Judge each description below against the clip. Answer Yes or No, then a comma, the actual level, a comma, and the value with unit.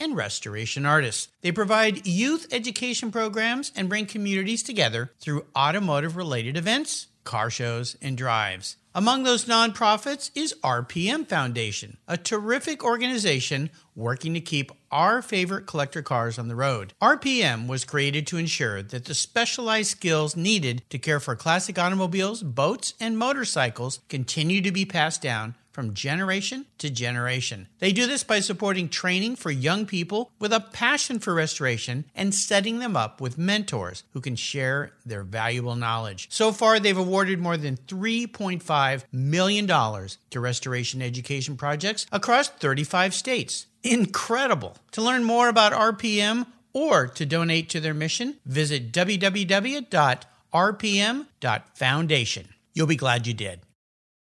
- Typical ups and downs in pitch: No, wide, 8.9 semitones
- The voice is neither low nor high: Yes, medium, 165 Hz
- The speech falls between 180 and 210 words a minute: No, average, 140 wpm